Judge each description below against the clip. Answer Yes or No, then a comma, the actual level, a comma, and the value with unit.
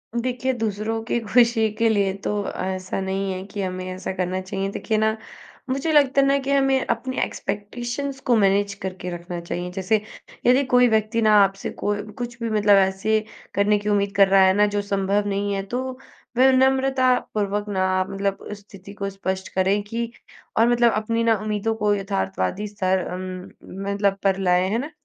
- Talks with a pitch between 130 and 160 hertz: No, high, 205 Hz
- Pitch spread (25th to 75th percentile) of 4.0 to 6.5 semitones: No, average, 3.3 semitones